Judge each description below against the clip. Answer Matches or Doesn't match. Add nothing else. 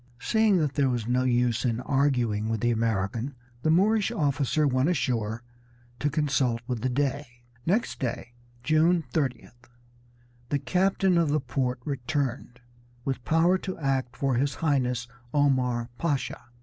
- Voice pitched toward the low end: Matches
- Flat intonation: Doesn't match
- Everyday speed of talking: Matches